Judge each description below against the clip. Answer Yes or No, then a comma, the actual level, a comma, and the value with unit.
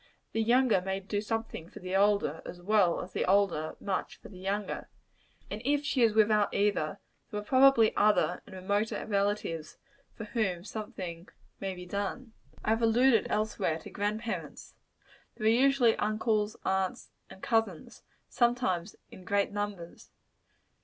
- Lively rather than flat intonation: No, average, 2.8 semitones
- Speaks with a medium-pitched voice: No, high, 205 Hz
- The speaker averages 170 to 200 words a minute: No, average, 155 wpm